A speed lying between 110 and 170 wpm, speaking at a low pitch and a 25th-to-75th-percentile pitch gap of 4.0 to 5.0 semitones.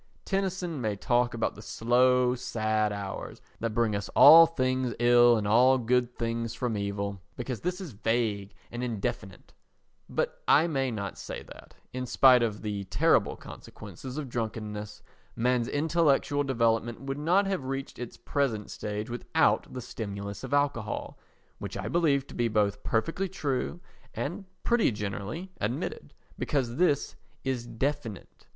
Yes: average, 145 wpm; low, 120 Hz; average, 4.3 semitones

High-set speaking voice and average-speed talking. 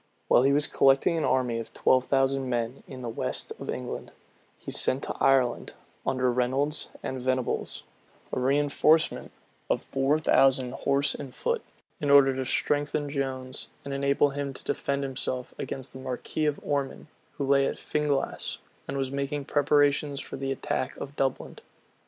No: low, 135 Hz; average, 165 wpm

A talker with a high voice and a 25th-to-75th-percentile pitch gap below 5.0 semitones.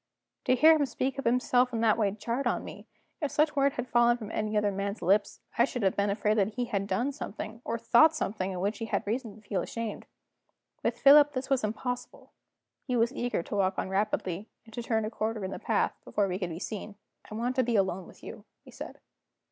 Yes: high, 225 Hz; average, 3.6 semitones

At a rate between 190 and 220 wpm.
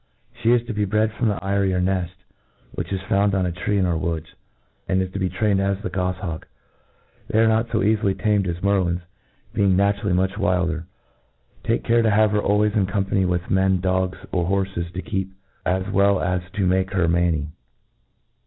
Yes: average, 200 wpm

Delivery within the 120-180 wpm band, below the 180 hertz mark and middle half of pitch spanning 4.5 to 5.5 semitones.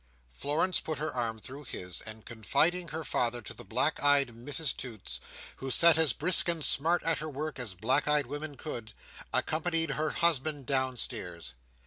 Yes: average, 170 wpm; medium, 140 Hz; average, 4.8 semitones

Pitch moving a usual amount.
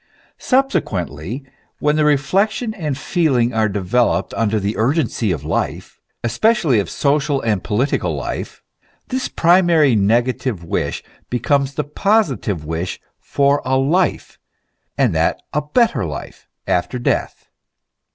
No: wide, 6.3 semitones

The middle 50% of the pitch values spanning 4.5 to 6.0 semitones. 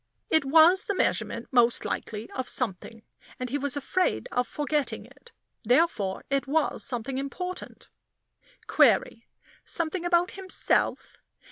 Yes: wide, 5.6 semitones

